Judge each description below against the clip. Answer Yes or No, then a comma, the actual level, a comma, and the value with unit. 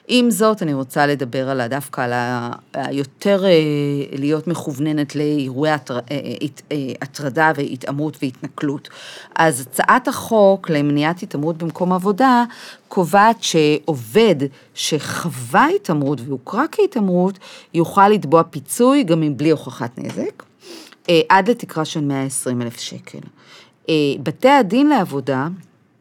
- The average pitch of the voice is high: No, medium, 155 Hz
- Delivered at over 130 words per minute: No, average, 105 wpm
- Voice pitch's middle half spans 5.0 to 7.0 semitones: Yes, average, 5.3 semitones